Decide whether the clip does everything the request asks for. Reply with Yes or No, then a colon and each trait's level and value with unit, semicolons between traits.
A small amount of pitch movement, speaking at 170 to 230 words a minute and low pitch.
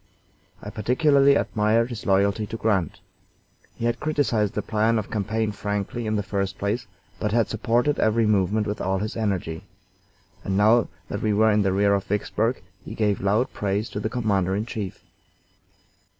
Yes: narrow, 2.2 semitones; average, 175 wpm; low, 105 Hz